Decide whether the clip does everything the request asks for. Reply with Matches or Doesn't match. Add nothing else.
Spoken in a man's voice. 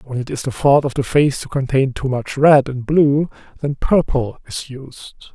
Matches